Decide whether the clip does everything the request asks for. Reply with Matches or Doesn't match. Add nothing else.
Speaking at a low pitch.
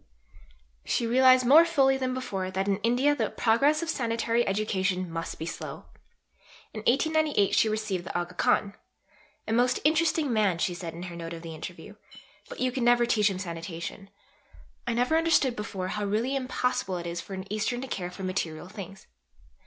Doesn't match